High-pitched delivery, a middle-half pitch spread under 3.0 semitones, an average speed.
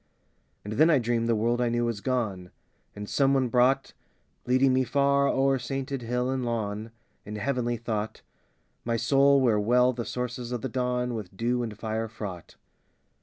No: low, 120 Hz; narrow, 2.6 semitones; average, 175 wpm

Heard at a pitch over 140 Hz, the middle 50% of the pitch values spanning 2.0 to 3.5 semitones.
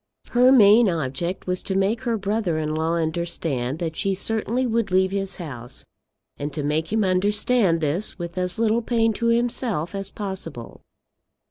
No: high, 190 Hz; average, 5.3 semitones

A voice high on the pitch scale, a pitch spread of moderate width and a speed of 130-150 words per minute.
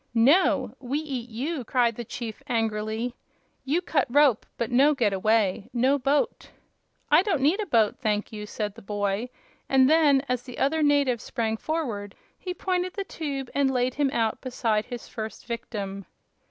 No: very high, 250 Hz; average, 4.6 semitones; average, 170 wpm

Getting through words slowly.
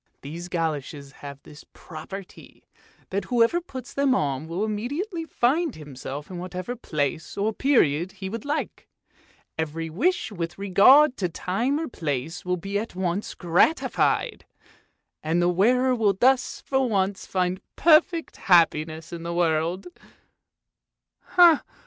Yes: slow, 130 wpm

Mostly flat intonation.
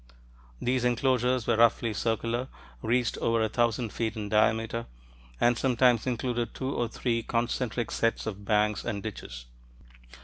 Yes: narrow, 1.7 semitones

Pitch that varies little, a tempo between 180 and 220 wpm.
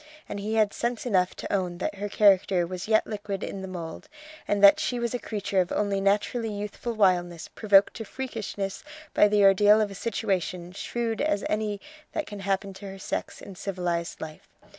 Yes: narrow, 2.1 semitones; average, 195 wpm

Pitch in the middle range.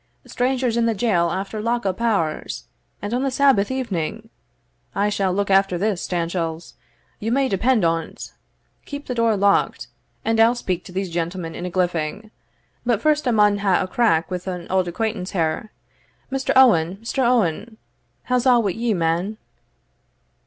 No: high, 205 Hz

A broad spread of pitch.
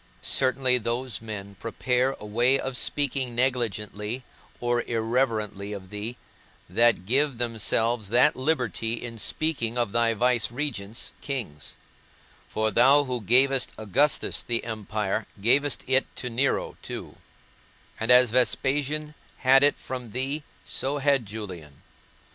No: average, 3.3 semitones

